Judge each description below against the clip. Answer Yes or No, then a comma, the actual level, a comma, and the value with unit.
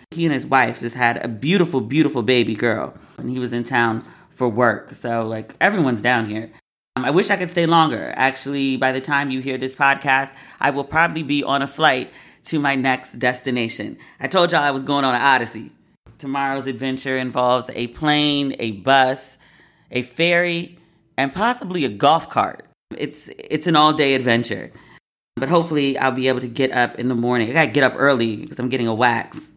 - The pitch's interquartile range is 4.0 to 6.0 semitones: No, average, 3.1 semitones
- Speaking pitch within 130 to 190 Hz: Yes, low, 135 Hz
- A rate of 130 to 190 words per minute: No, fast, 205 wpm